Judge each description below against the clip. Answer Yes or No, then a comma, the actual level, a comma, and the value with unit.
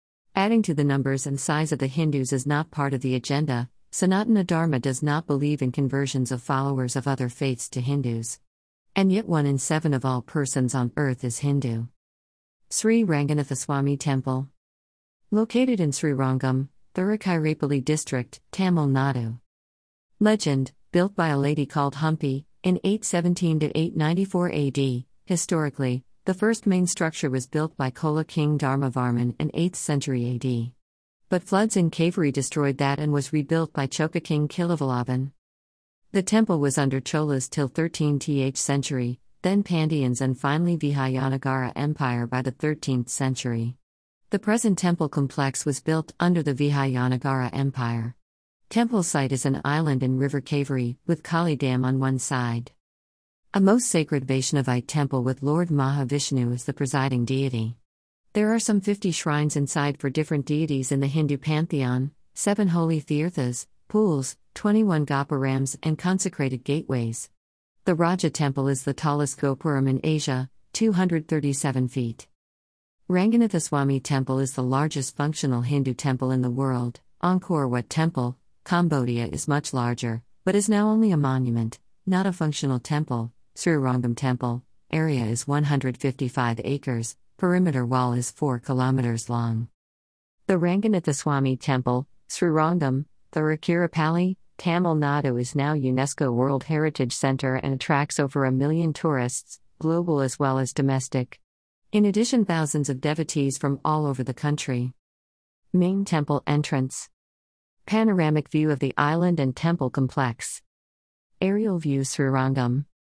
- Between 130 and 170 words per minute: Yes, average, 140 wpm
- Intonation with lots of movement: No, average, 3.6 semitones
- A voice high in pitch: No, medium, 140 Hz